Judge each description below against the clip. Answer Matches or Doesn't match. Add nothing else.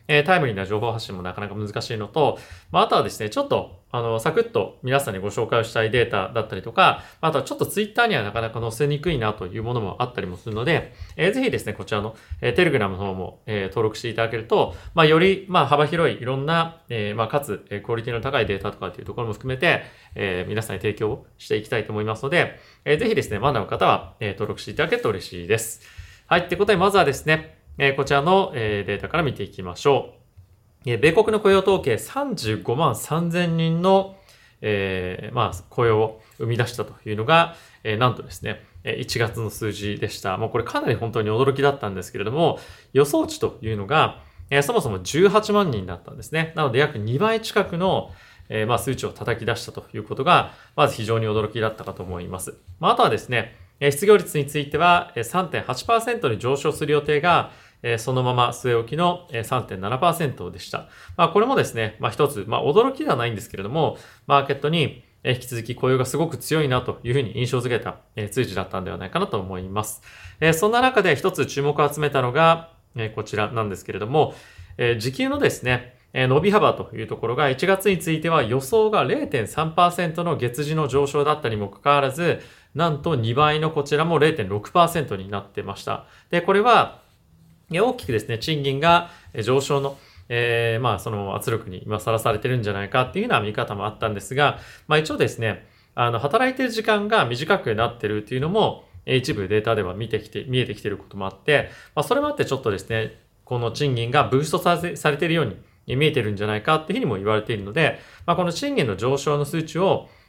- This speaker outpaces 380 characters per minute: Matches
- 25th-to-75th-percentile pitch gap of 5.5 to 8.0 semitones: Matches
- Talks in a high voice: Doesn't match